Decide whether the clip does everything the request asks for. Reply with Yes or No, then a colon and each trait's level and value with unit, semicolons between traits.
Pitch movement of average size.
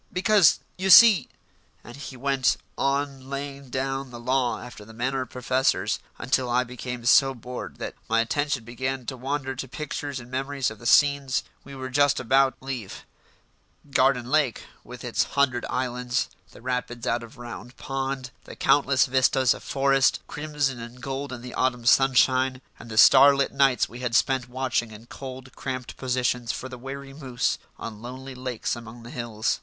No: narrow, 1.9 semitones